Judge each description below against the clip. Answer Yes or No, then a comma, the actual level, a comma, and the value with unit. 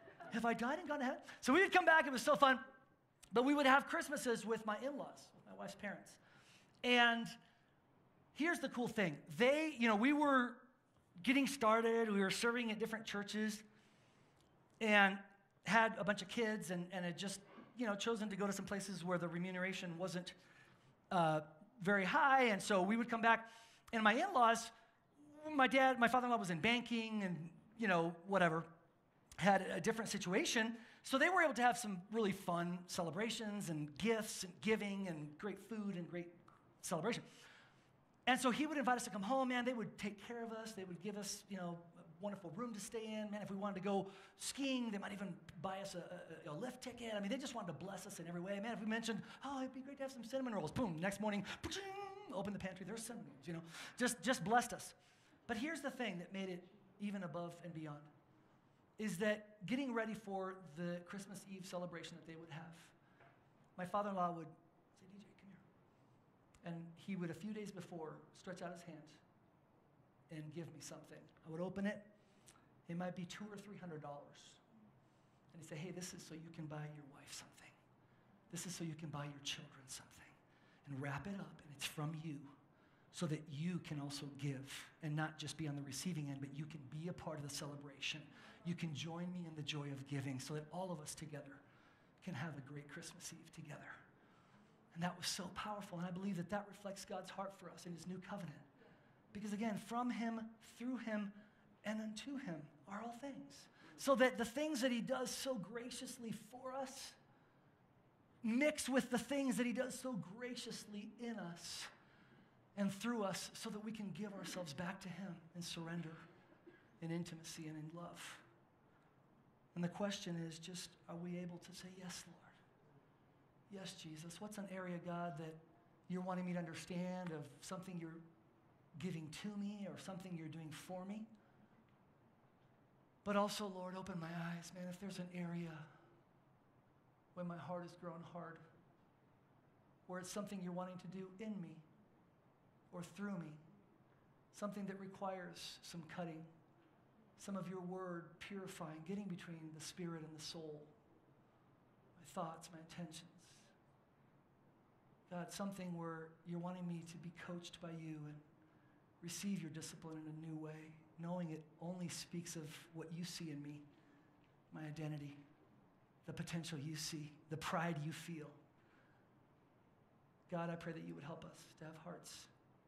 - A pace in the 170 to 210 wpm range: Yes, average, 190 wpm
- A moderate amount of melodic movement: Yes, average, 4.6 semitones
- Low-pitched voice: No, medium, 180 Hz